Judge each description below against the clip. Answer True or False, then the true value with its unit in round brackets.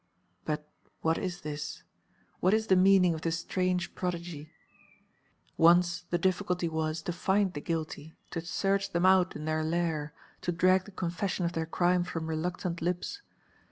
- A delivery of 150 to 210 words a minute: True (160 wpm)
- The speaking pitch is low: False (175 Hz)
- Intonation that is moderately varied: False (2.2 semitones)